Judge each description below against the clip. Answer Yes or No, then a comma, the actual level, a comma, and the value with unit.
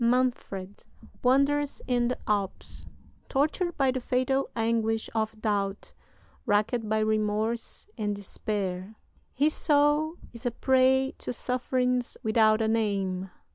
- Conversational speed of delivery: No, slow, 120 wpm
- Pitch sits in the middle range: No, high, 230 Hz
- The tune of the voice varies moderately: Yes, average, 3.4 semitones